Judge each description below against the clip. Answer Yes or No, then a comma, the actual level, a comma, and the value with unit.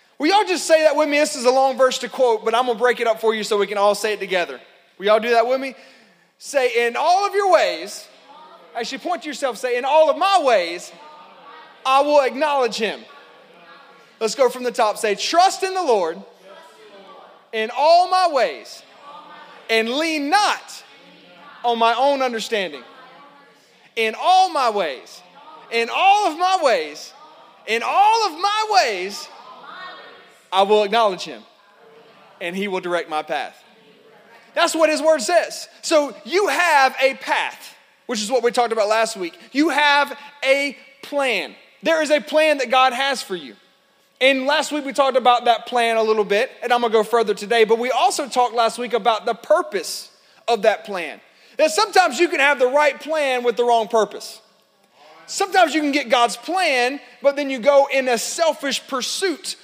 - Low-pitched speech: No, very high, 260 Hz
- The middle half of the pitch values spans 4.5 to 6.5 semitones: Yes, average, 5.1 semitones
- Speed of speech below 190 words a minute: No, average, 195 wpm